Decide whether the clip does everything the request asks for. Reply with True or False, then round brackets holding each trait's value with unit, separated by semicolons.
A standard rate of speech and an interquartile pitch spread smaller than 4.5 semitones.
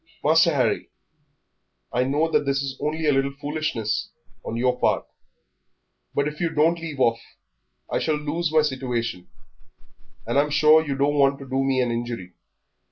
True (165 wpm; 3.3 semitones)